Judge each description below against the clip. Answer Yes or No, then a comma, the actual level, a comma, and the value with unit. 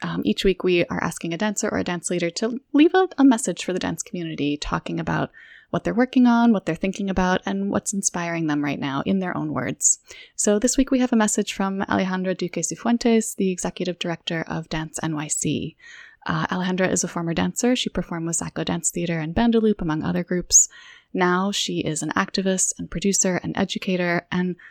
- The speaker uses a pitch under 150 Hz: No, medium, 185 Hz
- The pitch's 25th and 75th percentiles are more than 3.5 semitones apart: Yes, average, 4.1 semitones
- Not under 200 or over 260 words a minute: Yes, fast, 205 wpm